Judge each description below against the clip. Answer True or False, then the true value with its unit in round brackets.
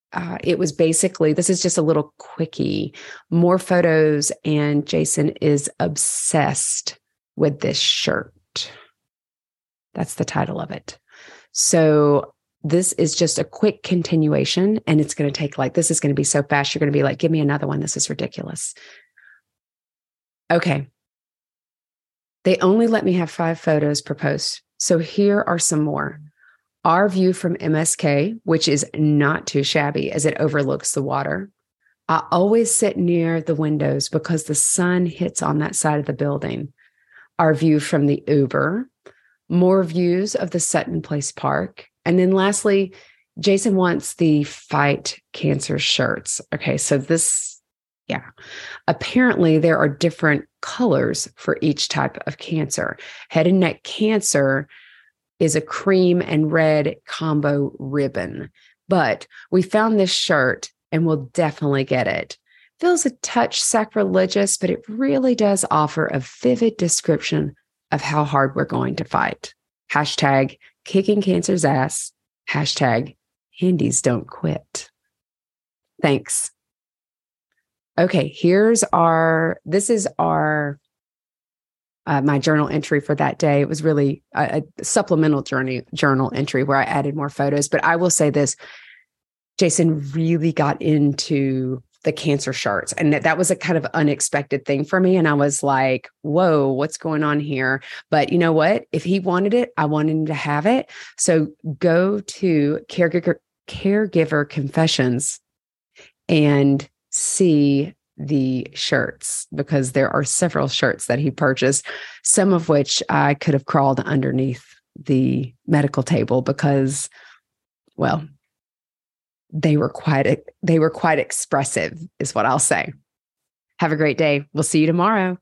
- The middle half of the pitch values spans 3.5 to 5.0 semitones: True (3.8 semitones)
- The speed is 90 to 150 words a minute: True (145 wpm)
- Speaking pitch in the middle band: True (155 Hz)